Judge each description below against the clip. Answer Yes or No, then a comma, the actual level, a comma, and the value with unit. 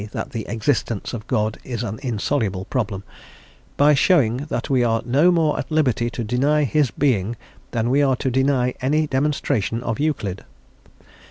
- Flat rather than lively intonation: No, average, 4.2 semitones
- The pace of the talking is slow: No, average, 165 wpm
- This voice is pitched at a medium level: No, low, 125 Hz